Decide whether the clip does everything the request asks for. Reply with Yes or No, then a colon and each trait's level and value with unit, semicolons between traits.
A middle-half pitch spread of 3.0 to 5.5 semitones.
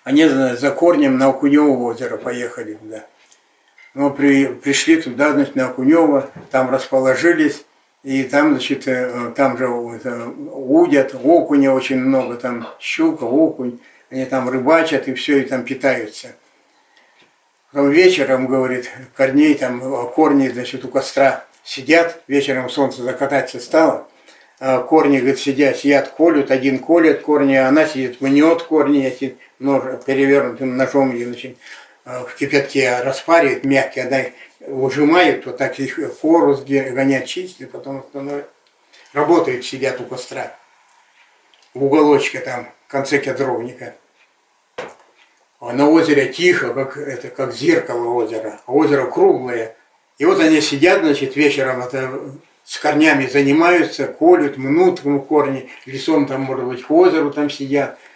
No: narrow, 2.5 semitones